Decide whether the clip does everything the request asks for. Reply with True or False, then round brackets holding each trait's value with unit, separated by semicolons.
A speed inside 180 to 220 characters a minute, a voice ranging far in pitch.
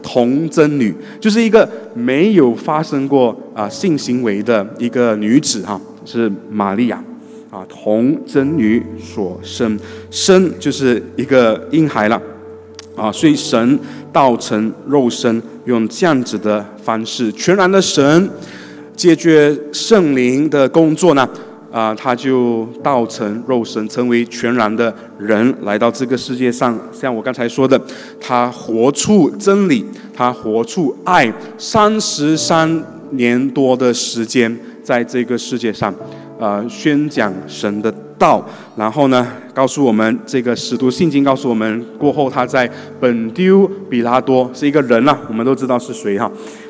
False (210 characters per minute; 4.8 semitones)